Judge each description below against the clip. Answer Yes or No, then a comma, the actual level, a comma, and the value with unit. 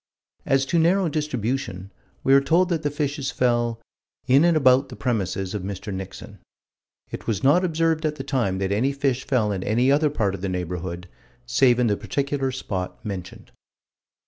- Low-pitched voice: Yes, low, 125 Hz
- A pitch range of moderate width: No, wide, 6.5 semitones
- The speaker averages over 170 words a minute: Yes, average, 180 wpm